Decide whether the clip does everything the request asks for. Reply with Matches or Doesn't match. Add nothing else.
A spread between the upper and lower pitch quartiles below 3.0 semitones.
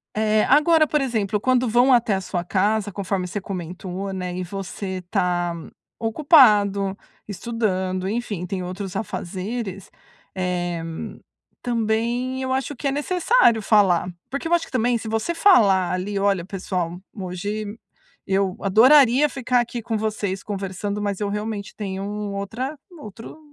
Doesn't match